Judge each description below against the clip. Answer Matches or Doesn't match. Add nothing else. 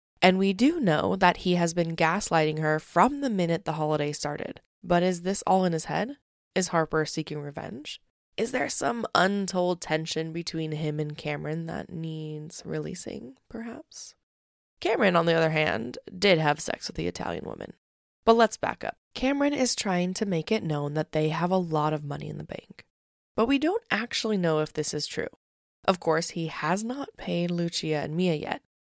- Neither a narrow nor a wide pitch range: Matches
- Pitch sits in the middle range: Matches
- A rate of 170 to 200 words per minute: Matches